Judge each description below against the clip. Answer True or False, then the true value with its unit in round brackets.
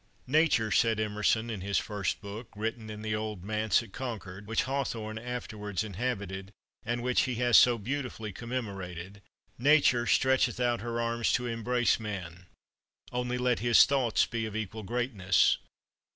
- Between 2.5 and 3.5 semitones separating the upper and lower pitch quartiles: True (2.9 semitones)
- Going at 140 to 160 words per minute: True (150 wpm)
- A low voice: True (110 Hz)